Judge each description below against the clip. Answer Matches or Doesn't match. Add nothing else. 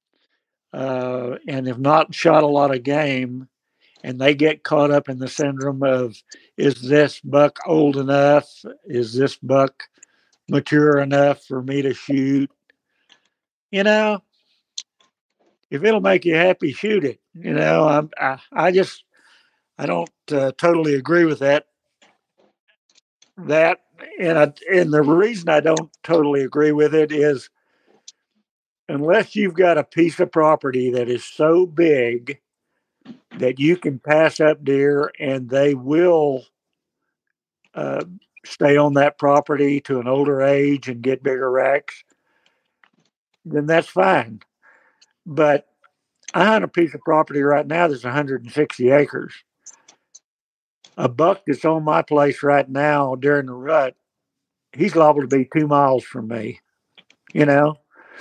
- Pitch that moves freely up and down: Doesn't match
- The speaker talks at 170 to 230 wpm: Doesn't match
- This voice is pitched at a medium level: Matches